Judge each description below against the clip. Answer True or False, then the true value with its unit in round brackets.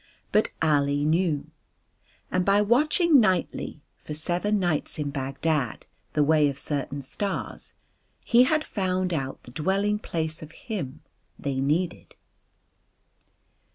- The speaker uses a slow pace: True (120 wpm)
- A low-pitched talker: False (160 Hz)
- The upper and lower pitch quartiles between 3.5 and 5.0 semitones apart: False (5.5 semitones)